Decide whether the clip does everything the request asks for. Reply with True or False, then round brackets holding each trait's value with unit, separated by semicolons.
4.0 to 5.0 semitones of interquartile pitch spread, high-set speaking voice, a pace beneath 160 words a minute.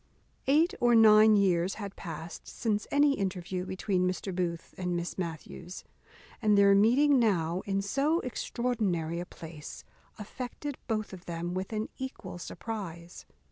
True (4.3 semitones; 195 Hz; 145 wpm)